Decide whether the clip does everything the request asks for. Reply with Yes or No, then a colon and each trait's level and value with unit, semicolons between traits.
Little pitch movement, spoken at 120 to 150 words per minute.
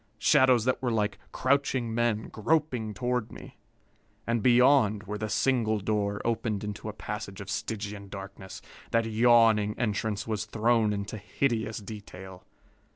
Yes: narrow, 2.3 semitones; average, 140 wpm